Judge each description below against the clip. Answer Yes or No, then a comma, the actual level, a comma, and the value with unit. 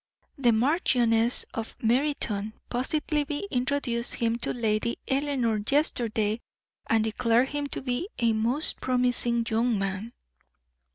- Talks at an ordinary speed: No, slow, 115 wpm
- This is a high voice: Yes, high, 240 Hz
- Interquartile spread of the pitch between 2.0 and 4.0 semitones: Yes, average, 3.4 semitones